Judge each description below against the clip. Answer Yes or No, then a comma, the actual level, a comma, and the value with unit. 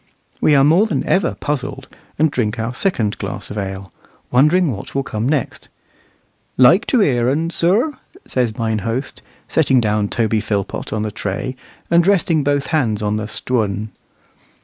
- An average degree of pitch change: No, wide, 6.2 semitones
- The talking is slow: No, average, 165 wpm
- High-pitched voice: No, low, 125 Hz